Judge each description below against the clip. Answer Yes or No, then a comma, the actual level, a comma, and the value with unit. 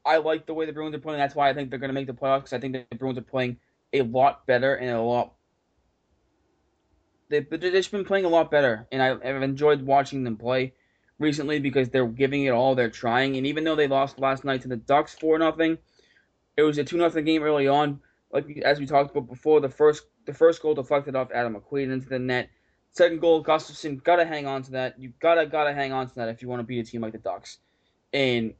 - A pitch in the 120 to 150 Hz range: Yes, medium, 140 Hz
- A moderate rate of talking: No, fast, 250 wpm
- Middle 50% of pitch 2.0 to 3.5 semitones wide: Yes, average, 2.9 semitones